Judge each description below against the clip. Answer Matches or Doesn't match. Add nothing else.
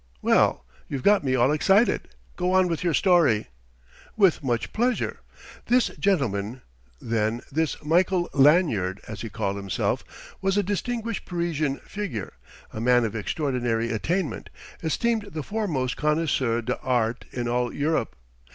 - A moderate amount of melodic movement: Doesn't match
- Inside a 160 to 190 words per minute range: Doesn't match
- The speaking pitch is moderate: Matches